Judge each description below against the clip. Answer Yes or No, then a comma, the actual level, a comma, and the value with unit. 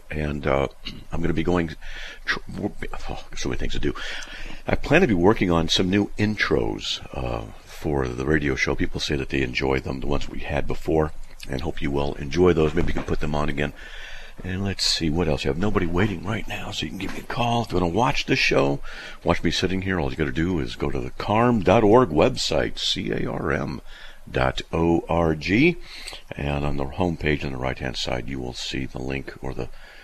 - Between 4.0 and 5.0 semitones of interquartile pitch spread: Yes, average, 4.6 semitones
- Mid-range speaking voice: No, very low, 80 Hz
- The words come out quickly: Yes, fast, 225 wpm